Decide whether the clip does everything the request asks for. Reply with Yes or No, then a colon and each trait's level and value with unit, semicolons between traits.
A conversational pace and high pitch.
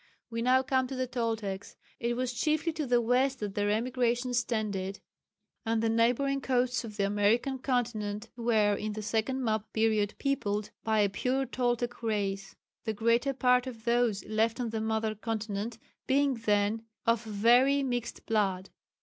Yes: average, 165 wpm; high, 230 Hz